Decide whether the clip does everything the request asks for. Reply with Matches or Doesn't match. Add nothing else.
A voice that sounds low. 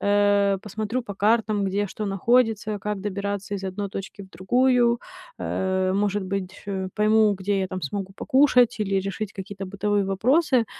Doesn't match